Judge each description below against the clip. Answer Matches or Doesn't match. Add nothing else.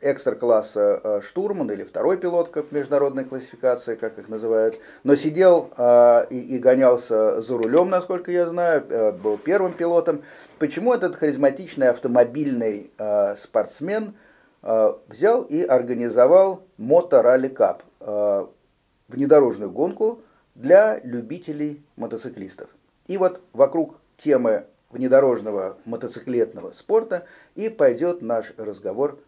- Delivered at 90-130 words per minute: Matches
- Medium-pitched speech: Matches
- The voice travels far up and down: Matches